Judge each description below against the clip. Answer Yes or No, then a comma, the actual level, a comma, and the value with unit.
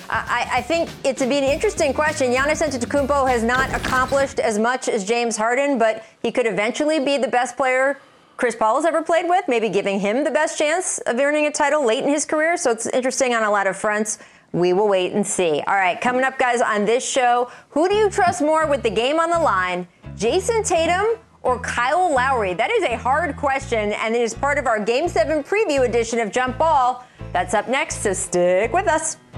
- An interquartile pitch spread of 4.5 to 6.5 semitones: Yes, average, 5.1 semitones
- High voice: Yes, very high, 265 Hz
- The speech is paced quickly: Yes, fast, 225 wpm